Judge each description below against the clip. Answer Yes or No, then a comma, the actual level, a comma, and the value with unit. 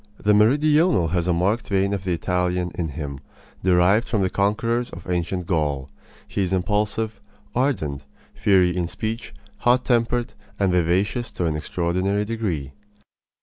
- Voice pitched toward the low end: Yes, very low, 95 Hz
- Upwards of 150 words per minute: No, average, 145 wpm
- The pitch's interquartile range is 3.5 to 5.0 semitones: Yes, average, 4.1 semitones